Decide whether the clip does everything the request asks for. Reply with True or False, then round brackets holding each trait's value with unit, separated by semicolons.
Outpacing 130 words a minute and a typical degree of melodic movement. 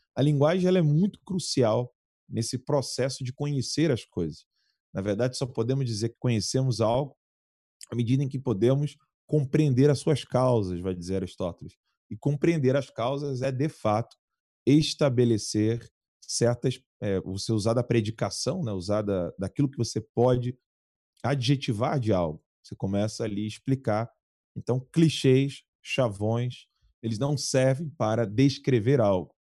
True (145 wpm; 4.3 semitones)